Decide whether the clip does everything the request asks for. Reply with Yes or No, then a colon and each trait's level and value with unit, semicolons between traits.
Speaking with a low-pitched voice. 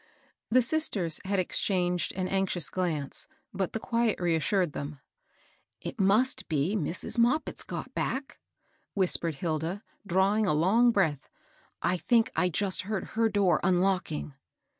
No: medium, 185 Hz